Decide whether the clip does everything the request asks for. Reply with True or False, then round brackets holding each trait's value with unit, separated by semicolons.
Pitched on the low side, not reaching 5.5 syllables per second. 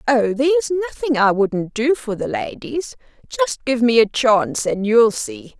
False (240 Hz; 4.8 syllables/s)